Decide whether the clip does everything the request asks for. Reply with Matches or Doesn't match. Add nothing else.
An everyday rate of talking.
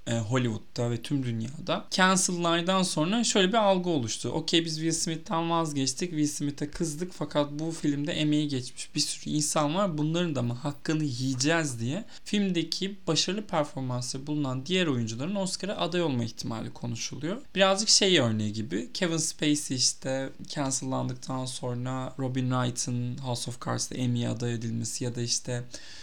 Doesn't match